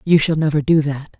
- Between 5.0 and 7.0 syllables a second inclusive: Yes, 5.5 syllables/s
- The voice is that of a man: No, female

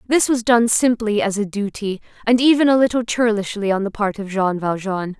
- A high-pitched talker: Yes, high, 215 Hz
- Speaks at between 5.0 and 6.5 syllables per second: Yes, 5.2 syllables/s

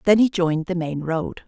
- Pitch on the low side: No, medium, 175 Hz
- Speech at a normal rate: No, fast, 245 wpm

